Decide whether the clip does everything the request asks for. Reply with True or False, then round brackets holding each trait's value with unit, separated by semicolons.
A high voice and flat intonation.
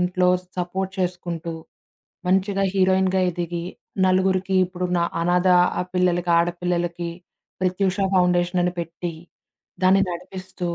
False (180 Hz; 1.2 semitones)